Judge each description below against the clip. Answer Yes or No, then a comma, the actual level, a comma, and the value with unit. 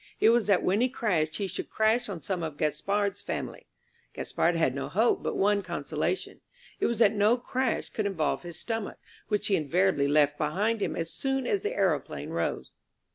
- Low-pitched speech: No, high, 200 Hz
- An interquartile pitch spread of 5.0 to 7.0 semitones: Yes, wide, 5.4 semitones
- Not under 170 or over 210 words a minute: Yes, average, 190 wpm